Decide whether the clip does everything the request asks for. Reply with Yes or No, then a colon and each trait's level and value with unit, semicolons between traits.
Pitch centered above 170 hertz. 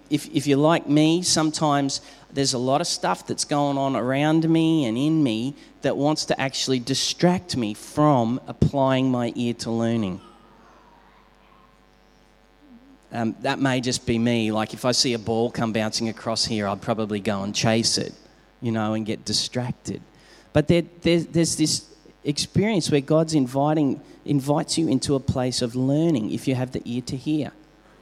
No: low, 135 Hz